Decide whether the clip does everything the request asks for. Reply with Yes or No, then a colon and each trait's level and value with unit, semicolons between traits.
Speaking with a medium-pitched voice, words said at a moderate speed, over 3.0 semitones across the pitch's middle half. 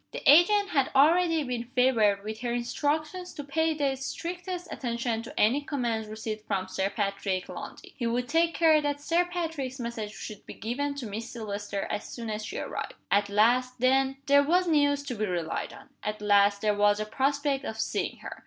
No: very high, 250 Hz; average, 195 wpm; average, 5.3 semitones